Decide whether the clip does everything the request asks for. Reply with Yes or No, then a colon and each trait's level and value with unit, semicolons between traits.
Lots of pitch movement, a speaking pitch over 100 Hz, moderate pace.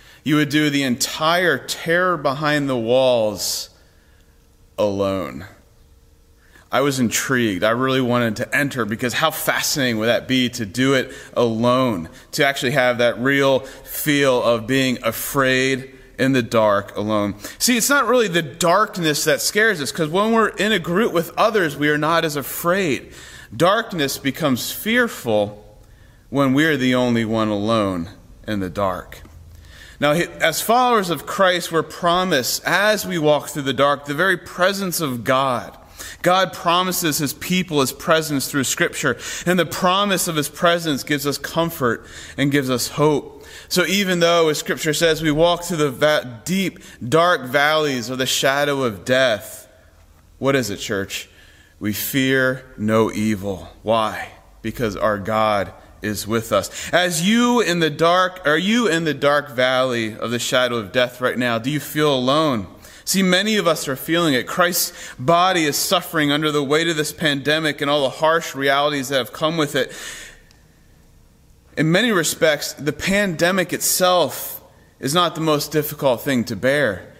Yes: wide, 6.1 semitones; medium, 140 Hz; average, 165 wpm